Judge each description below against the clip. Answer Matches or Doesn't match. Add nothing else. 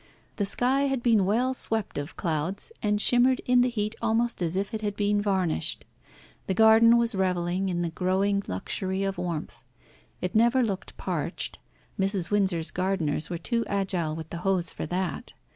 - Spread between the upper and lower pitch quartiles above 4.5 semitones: Doesn't match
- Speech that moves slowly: Doesn't match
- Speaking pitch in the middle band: Doesn't match